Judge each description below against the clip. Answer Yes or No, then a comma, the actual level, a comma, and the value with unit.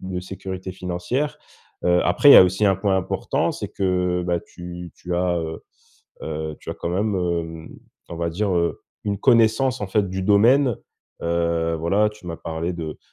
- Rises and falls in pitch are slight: No, average, 3.0 semitones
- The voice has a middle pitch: No, very low, 90 Hz